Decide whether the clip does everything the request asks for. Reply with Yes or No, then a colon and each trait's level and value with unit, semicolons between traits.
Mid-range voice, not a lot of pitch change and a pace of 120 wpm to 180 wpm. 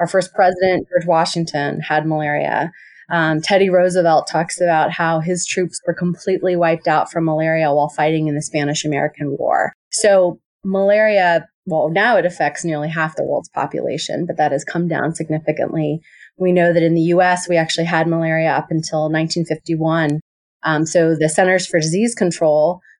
Yes: medium, 165 Hz; narrow, 2.3 semitones; average, 170 wpm